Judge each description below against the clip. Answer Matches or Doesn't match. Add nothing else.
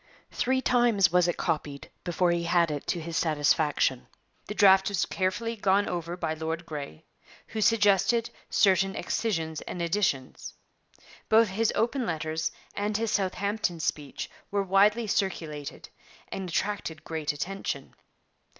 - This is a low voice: Doesn't match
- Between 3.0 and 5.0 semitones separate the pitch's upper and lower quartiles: Matches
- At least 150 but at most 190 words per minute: Doesn't match